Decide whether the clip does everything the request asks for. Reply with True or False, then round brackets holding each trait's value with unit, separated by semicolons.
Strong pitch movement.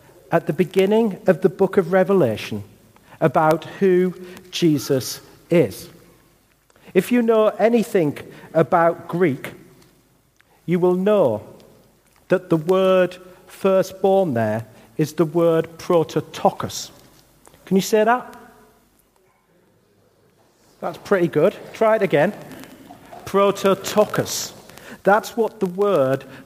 False (3.3 semitones)